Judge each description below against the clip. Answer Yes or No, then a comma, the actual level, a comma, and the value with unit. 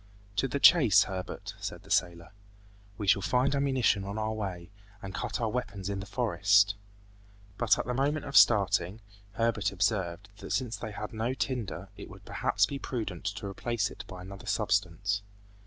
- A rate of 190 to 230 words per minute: No, average, 175 wpm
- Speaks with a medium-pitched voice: No, low, 105 Hz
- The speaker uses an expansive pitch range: No, average, 3.5 semitones